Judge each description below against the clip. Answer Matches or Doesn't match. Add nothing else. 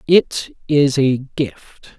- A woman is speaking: Doesn't match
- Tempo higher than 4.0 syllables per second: Doesn't match